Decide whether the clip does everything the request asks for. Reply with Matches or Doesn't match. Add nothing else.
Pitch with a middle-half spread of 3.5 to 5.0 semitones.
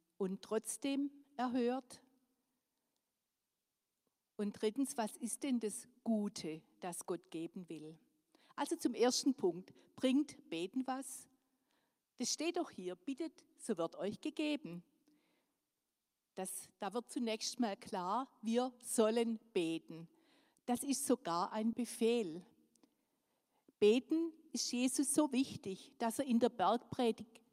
Matches